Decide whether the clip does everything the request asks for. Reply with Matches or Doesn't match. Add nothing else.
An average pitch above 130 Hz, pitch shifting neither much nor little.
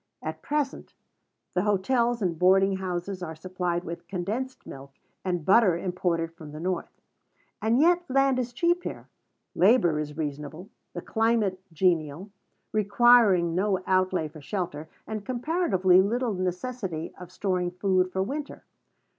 Matches